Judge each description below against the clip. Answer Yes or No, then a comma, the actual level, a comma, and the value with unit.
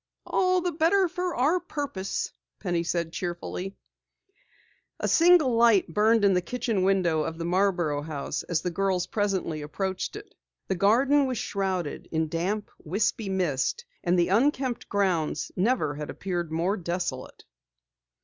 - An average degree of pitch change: No, wide, 5.7 semitones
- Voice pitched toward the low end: No, high, 190 Hz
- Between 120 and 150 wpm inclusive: Yes, average, 145 wpm